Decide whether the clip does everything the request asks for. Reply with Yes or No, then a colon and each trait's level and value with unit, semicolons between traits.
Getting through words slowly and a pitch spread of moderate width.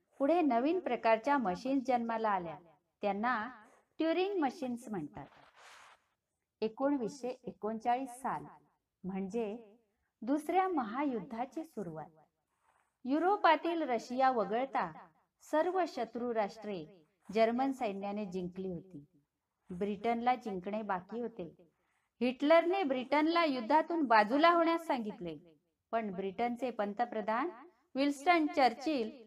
No: slow, 75 wpm; wide, 5.9 semitones